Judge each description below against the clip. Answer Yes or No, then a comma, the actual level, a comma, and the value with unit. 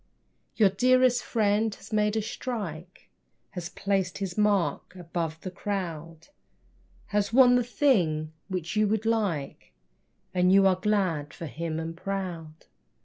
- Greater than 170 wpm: No, average, 140 wpm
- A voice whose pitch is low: No, high, 195 Hz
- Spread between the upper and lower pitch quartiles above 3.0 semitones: Yes, average, 4.2 semitones